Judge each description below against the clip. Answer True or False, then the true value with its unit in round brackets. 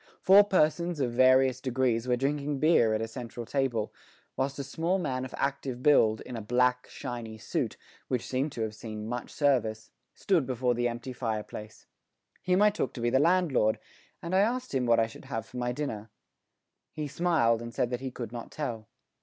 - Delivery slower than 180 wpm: False (195 wpm)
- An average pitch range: True (3.7 semitones)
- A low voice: True (125 Hz)